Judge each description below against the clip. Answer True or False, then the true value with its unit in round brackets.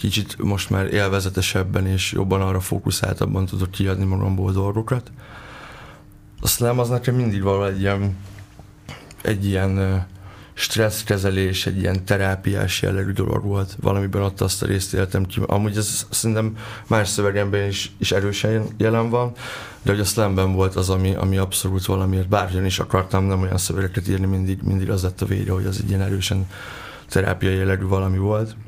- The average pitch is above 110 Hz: False (100 Hz)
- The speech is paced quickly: True (160 wpm)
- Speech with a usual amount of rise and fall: False (1.9 semitones)